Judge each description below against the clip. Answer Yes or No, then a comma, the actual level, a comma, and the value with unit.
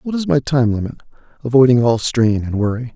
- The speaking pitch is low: Yes, low, 125 Hz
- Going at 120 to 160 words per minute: No, fast, 205 wpm